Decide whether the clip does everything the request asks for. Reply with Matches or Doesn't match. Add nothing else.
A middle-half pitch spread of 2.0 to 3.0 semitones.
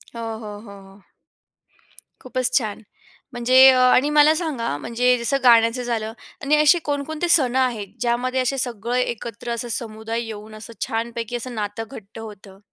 Matches